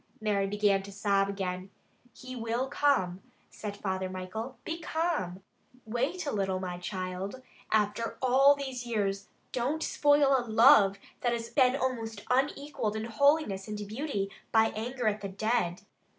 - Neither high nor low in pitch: No, high, 220 Hz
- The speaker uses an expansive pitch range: No, average, 4.7 semitones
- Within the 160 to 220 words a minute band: No, average, 150 wpm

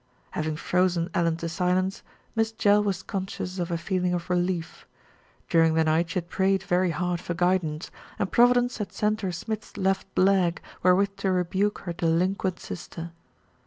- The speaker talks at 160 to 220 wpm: Yes, average, 170 wpm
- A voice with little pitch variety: Yes, narrow, 2.2 semitones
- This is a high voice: No, medium, 180 Hz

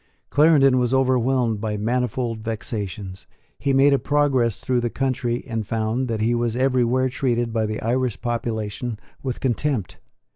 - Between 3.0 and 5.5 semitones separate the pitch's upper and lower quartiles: No, narrow, 2.6 semitones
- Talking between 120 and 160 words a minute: Yes, average, 150 wpm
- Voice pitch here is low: Yes, low, 120 Hz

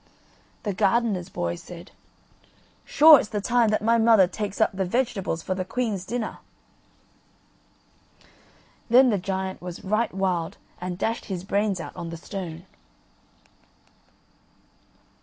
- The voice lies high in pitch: Yes, high, 195 Hz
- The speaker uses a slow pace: Yes, slow, 130 wpm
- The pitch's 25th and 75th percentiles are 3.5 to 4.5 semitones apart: Yes, average, 3.9 semitones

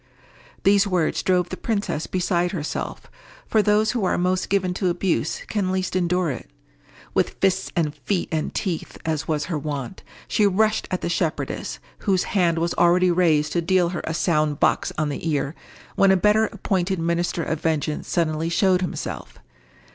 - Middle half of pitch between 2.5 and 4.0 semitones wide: Yes, average, 2.8 semitones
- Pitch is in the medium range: Yes, medium, 175 Hz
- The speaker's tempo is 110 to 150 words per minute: No, average, 175 wpm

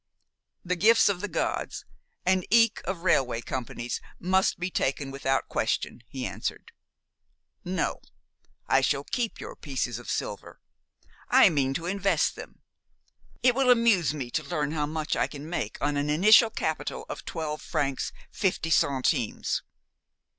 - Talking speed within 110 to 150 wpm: Yes, average, 145 wpm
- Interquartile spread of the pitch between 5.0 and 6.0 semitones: Yes, wide, 5.6 semitones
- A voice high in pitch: No, medium, 160 Hz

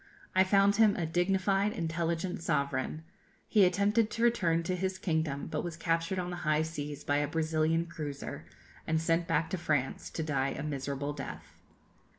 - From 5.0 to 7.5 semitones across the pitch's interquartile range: No, average, 3.5 semitones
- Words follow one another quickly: No, average, 170 wpm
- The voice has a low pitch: No, medium, 165 Hz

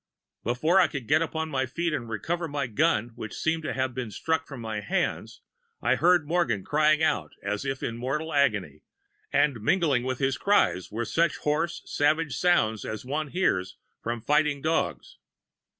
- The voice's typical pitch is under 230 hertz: Yes, medium, 140 Hz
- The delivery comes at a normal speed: Yes, average, 175 wpm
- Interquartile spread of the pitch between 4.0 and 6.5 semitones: Yes, wide, 5.4 semitones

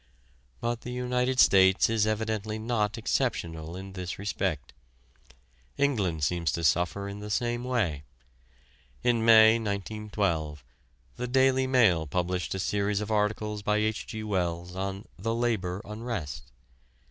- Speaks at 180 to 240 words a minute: No, slow, 135 wpm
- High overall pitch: No, low, 105 Hz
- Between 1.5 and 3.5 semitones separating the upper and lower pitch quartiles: No, average, 3.9 semitones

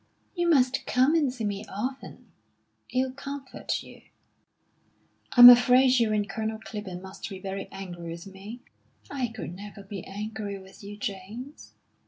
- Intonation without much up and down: No, average, 4.6 semitones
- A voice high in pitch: Yes, high, 215 Hz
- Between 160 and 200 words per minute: No, average, 150 wpm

